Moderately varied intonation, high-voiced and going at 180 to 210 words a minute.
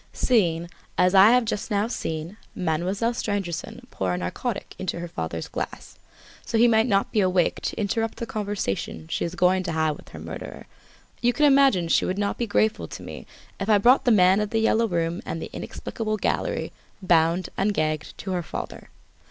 Yes: average, 4.7 semitones; high, 195 Hz; average, 200 wpm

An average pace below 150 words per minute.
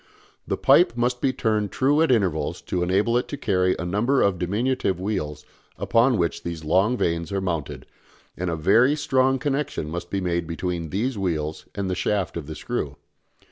No: average, 185 wpm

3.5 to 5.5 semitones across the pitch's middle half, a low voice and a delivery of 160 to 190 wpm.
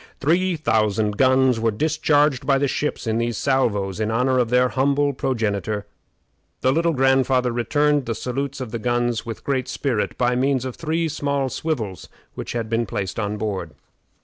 Yes: average, 3.9 semitones; low, 125 Hz; average, 175 wpm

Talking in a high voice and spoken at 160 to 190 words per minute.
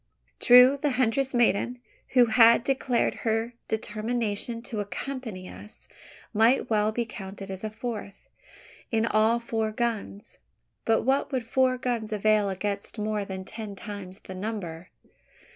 No: high, 220 Hz; average, 140 wpm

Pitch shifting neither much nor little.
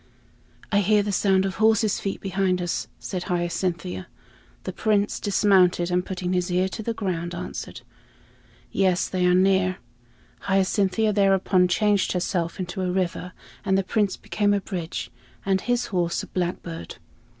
No: narrow, 1.9 semitones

